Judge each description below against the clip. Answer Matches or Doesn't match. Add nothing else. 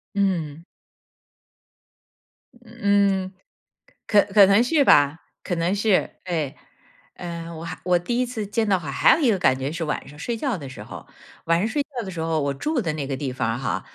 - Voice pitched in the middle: Matches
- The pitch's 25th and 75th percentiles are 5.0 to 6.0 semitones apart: Matches